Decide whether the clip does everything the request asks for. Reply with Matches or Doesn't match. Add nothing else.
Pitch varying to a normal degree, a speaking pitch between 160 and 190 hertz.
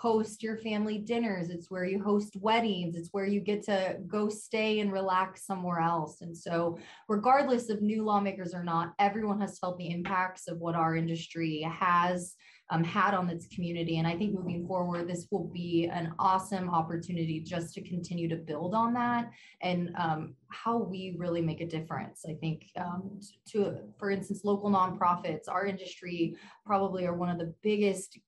Matches